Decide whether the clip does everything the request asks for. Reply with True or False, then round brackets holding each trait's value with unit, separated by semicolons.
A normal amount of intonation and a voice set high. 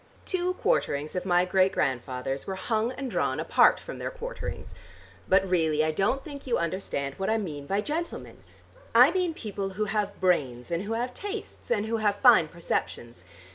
False (7.0 semitones; 195 Hz)